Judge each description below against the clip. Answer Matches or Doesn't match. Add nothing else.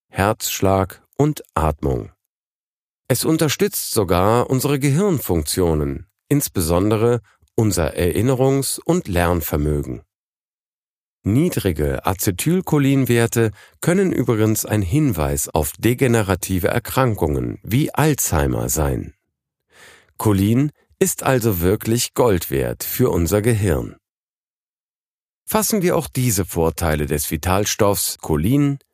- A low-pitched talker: Matches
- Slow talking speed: Matches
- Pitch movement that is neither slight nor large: Doesn't match